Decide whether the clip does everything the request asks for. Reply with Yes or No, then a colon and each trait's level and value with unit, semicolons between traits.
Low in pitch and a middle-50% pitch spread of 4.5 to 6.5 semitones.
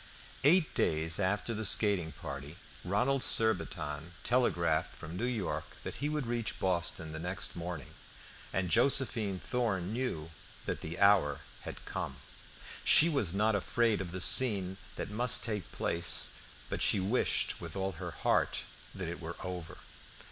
Yes: very low, 95 Hz; average, 5.2 semitones